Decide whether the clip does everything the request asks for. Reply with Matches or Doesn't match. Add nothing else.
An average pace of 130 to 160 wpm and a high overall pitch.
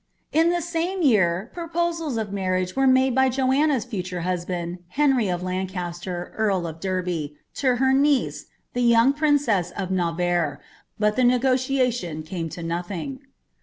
Matches